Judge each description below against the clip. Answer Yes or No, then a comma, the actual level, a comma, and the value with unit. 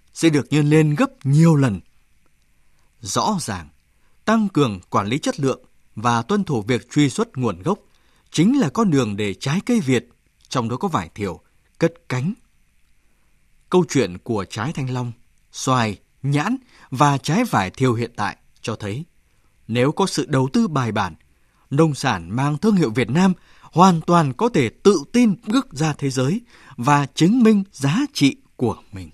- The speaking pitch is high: No, medium, 140 Hz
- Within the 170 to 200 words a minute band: Yes, average, 175 wpm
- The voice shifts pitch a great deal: Yes, wide, 6.3 semitones